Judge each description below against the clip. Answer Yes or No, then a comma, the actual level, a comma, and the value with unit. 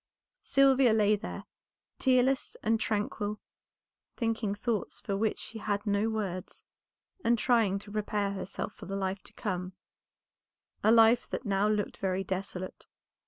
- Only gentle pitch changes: Yes, narrow, 2.3 semitones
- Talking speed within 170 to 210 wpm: No, average, 140 wpm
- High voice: Yes, high, 210 Hz